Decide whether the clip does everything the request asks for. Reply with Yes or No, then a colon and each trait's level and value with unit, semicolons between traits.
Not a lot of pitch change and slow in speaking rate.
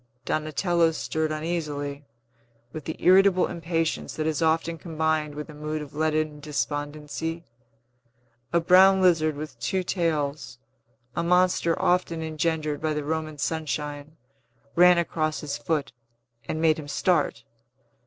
Yes: narrow, 1.9 semitones; slow, 130 wpm